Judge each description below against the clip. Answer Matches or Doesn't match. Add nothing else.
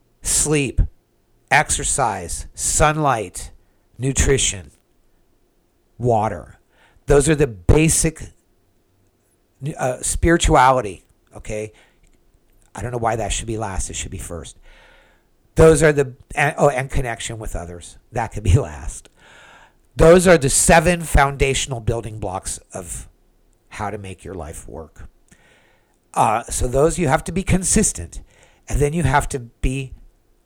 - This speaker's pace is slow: Matches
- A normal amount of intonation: Doesn't match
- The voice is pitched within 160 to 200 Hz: Doesn't match